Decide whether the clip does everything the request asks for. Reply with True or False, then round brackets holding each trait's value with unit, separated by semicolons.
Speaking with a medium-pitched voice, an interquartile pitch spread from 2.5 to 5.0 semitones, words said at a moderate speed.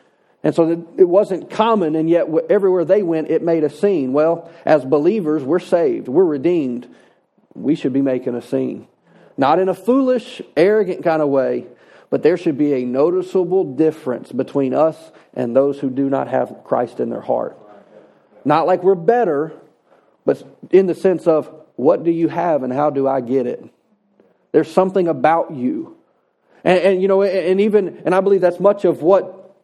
True (170 Hz; 4.3 semitones; 180 wpm)